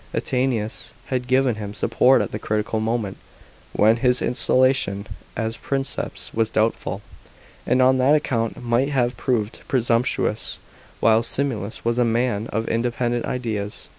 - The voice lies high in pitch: No, low, 120 Hz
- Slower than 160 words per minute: Yes, slow, 135 wpm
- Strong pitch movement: No, narrow, 2.5 semitones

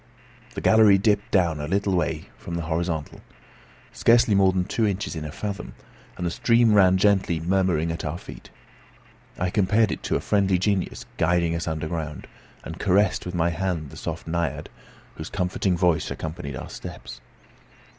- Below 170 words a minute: No, average, 175 wpm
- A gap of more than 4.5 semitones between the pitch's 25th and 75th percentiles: No, average, 3.2 semitones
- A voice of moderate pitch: No, very low, 90 Hz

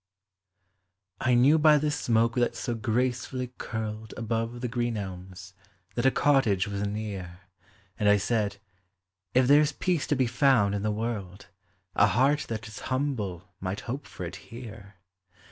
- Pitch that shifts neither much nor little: Yes, average, 4.1 semitones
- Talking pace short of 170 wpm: Yes, average, 160 wpm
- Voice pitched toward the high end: No, low, 115 Hz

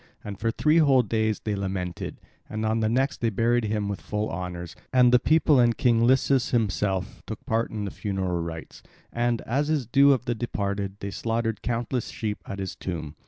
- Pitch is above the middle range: No, low, 110 Hz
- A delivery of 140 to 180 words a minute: No, fast, 205 wpm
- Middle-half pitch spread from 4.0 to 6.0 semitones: No, average, 3.5 semitones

